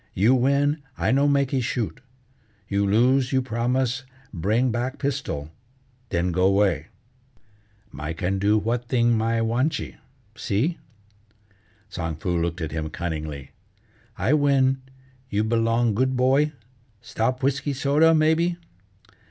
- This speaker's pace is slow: Yes, slow, 125 wpm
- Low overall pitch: Yes, low, 120 Hz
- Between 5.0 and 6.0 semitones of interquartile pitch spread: Yes, wide, 5.5 semitones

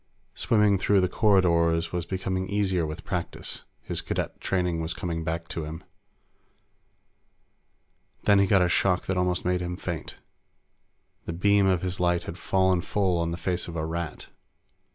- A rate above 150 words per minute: Yes, average, 165 wpm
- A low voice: Yes, very low, 90 Hz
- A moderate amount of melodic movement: No, narrow, 2.1 semitones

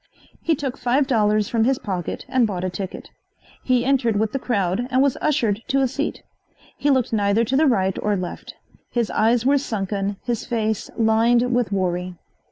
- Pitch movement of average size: Yes, average, 4.2 semitones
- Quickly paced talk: No, average, 185 wpm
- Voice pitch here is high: Yes, high, 230 Hz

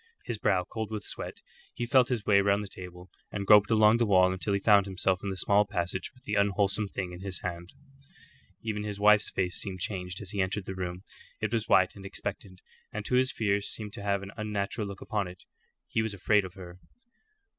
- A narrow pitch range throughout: Yes, narrow, 2.2 semitones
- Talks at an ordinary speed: No, fast, 220 wpm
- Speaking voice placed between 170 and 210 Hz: No, low, 100 Hz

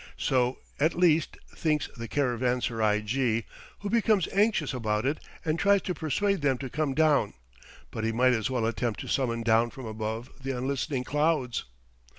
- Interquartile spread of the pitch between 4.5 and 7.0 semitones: Yes, average, 4.9 semitones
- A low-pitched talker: Yes, low, 130 Hz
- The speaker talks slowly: No, average, 165 wpm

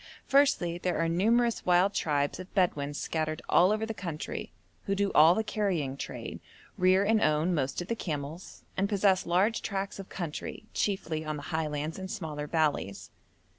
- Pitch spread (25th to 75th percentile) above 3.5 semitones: Yes, average, 4.4 semitones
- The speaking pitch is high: No, medium, 175 Hz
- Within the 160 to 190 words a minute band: Yes, average, 170 wpm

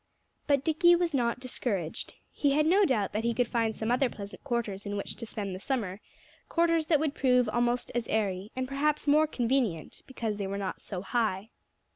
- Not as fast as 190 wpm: No, average, 200 wpm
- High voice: Yes, high, 240 Hz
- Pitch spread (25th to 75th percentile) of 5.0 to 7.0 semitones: Yes, average, 5.3 semitones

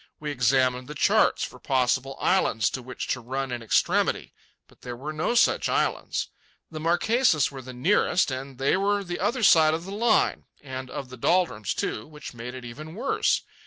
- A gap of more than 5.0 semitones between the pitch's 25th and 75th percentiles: Yes, wide, 5.5 semitones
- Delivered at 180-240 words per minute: Yes, average, 190 wpm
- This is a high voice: No, low, 135 Hz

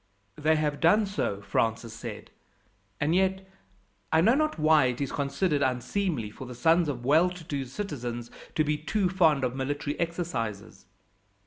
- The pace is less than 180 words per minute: Yes, average, 160 wpm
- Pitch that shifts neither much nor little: No, wide, 5.7 semitones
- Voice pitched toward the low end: No, medium, 150 Hz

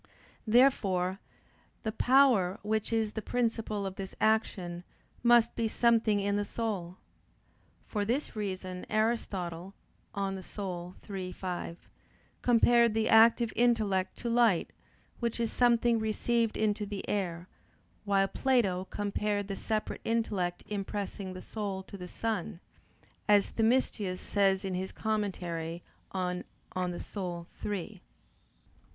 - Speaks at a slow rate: Yes, slow, 120 wpm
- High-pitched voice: Yes, high, 205 Hz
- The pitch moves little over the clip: No, average, 3.3 semitones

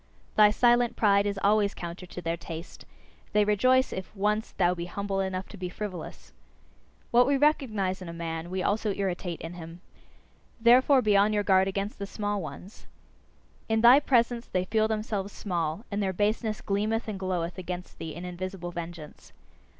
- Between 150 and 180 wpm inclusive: Yes, average, 175 wpm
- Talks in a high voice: Yes, high, 200 Hz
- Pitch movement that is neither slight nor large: Yes, average, 3.3 semitones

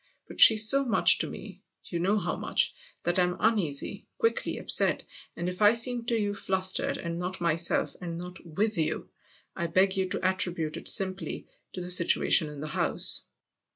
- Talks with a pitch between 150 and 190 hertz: Yes, medium, 185 Hz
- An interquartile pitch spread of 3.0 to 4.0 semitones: Yes, average, 3.3 semitones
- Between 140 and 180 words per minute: No, average, 200 wpm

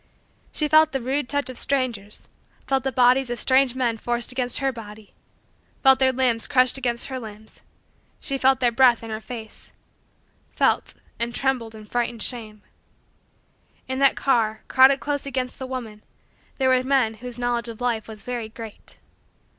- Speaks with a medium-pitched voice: No, high, 245 Hz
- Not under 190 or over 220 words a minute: No, average, 165 wpm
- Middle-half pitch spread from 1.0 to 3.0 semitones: Yes, narrow, 2.6 semitones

